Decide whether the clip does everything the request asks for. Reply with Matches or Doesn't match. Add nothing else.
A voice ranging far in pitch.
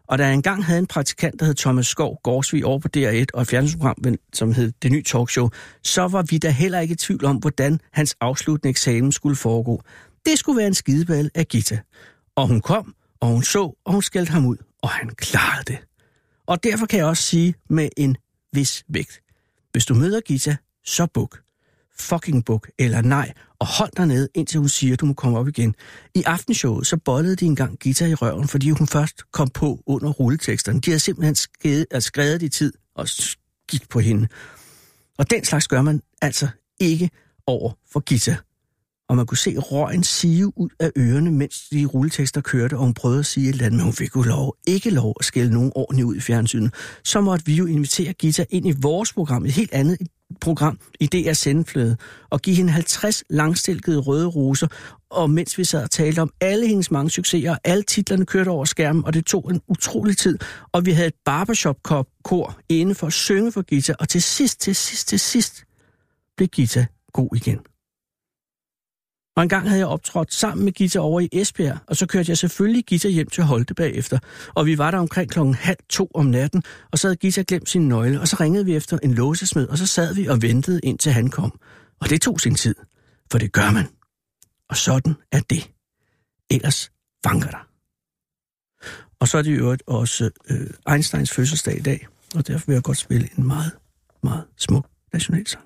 Doesn't match